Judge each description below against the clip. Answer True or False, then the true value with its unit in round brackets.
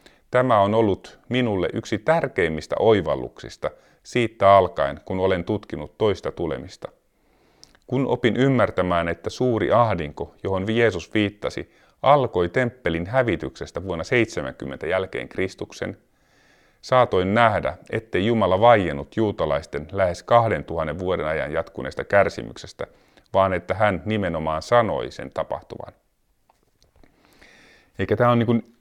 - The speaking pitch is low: True (100 Hz)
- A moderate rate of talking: True (110 wpm)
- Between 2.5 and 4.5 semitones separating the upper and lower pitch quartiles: False (5.0 semitones)